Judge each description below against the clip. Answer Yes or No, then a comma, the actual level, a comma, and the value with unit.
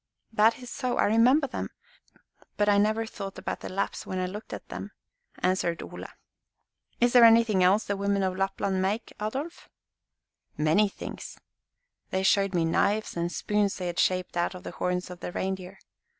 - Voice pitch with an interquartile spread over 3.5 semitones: No, average, 2.9 semitones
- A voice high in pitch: Yes, high, 195 Hz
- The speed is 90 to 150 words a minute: No, average, 180 wpm